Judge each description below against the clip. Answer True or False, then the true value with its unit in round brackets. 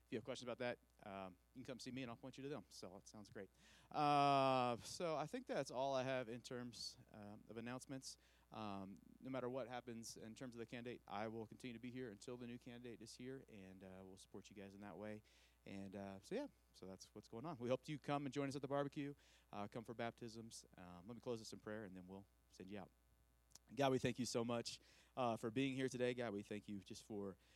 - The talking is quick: True (260 wpm)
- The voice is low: True (115 Hz)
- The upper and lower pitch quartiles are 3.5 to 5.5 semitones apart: True (4.5 semitones)